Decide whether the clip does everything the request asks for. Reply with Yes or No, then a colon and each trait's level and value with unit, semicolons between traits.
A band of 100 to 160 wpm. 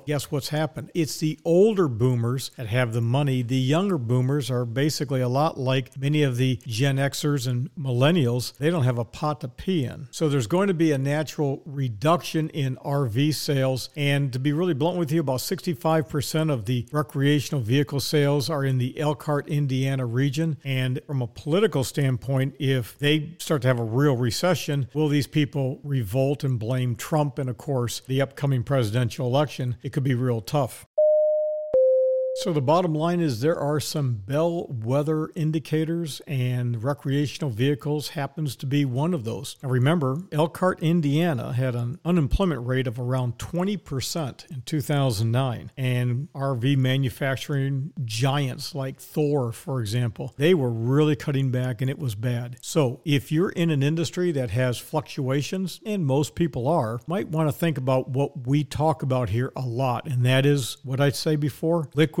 No: average, 175 wpm